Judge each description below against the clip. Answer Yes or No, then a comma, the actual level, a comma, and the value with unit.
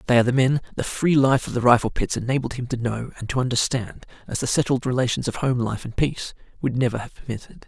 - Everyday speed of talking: No, fast, 240 wpm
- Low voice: Yes, low, 125 Hz